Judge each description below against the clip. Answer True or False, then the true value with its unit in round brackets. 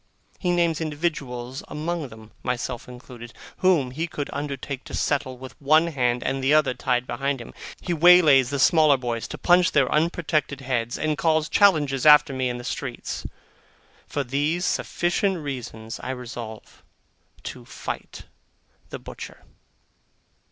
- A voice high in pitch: False (140 Hz)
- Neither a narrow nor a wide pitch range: True (4.0 semitones)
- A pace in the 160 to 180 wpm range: False (150 wpm)